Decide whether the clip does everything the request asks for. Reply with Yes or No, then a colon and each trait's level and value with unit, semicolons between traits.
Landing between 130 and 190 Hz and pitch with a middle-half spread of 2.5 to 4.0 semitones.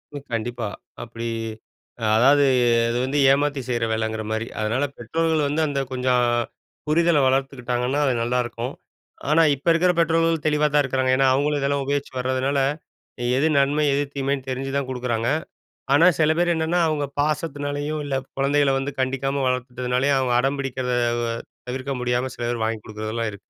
Yes: low, 135 Hz; average, 2.8 semitones